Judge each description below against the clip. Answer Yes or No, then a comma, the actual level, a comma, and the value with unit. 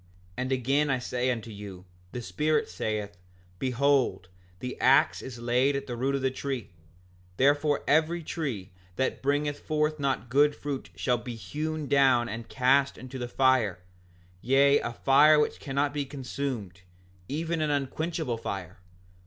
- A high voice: No, low, 135 Hz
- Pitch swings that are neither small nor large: Yes, average, 3.2 semitones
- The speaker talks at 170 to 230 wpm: No, average, 155 wpm